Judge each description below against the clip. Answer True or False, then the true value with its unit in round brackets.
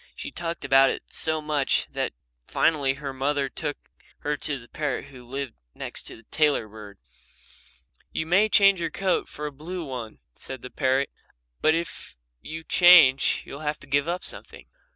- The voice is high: False (145 Hz)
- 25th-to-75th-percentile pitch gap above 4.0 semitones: False (3.2 semitones)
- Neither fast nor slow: True (175 wpm)